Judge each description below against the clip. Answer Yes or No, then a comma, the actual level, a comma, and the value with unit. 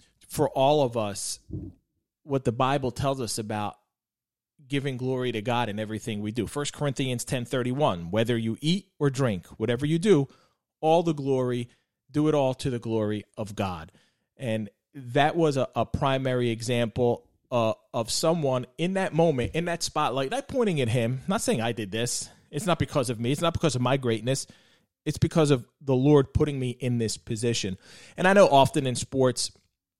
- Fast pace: No, average, 185 wpm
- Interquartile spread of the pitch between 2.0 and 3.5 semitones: No, average, 4.2 semitones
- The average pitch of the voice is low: Yes, low, 130 Hz